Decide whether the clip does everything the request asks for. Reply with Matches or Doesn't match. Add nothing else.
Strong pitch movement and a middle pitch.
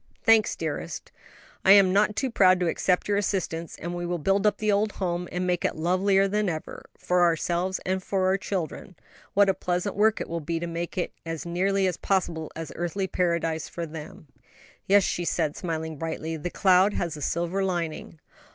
Doesn't match